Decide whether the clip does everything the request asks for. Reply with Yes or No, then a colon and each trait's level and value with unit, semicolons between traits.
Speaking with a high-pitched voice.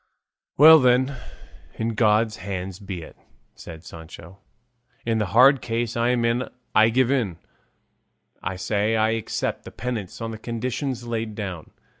No: low, 115 Hz